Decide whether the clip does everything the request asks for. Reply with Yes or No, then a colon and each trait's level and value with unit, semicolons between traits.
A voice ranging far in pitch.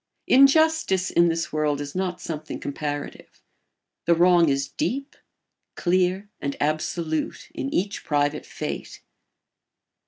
No: average, 4.2 semitones